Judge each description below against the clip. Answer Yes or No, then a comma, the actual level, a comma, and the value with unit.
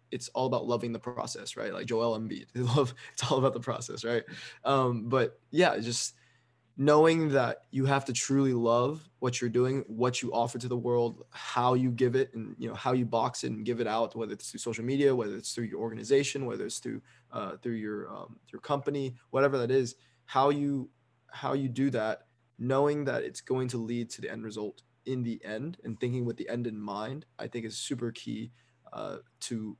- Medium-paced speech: No, fast, 215 wpm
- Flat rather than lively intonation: Yes, narrow, 2.3 semitones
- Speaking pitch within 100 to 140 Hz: Yes, low, 125 Hz